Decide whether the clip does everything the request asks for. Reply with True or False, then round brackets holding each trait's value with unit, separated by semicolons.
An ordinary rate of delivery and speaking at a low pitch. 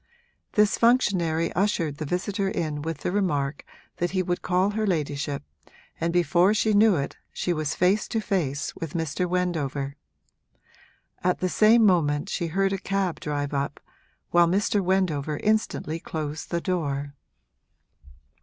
False (145 wpm; 175 Hz)